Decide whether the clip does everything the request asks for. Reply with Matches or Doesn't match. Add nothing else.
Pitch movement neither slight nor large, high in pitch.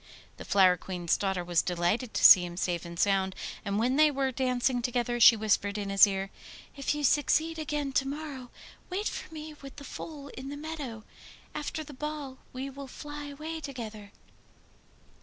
Doesn't match